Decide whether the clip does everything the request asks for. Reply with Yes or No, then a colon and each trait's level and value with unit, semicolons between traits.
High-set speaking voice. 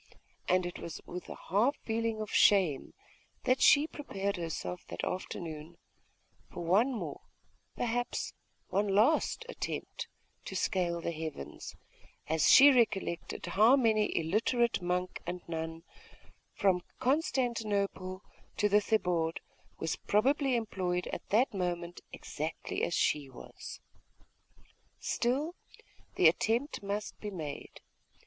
Yes: high, 195 Hz